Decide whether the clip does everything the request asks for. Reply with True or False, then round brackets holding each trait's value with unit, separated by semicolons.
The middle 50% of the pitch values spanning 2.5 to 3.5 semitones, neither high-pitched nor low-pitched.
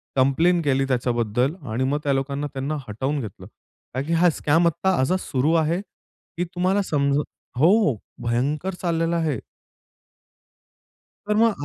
False (4.4 semitones; 145 Hz)